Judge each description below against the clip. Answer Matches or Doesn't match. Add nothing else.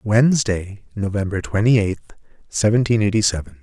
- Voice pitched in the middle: Doesn't match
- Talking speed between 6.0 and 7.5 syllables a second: Doesn't match